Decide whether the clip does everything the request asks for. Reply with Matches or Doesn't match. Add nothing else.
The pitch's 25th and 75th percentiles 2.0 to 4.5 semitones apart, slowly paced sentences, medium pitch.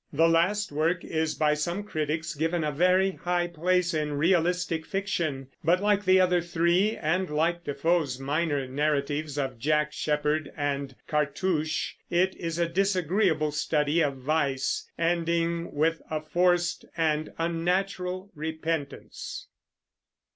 Matches